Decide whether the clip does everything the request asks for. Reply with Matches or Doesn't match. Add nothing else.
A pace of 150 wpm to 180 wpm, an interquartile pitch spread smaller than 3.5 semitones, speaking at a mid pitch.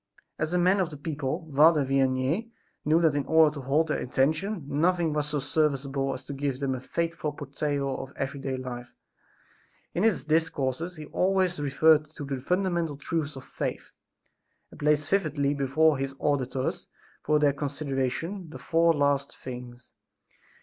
Matches